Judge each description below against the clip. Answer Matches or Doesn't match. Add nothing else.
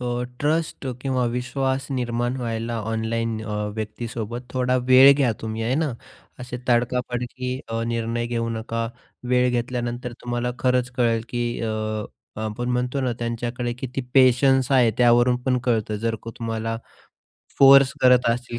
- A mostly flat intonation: Matches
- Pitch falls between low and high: Doesn't match